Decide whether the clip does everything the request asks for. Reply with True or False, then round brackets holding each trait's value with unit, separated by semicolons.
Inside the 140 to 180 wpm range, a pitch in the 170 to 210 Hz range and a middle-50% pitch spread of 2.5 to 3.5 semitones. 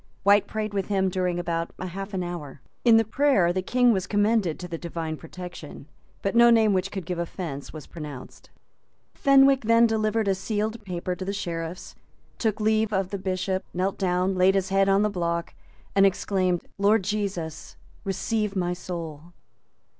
True (175 wpm; 190 Hz; 3.2 semitones)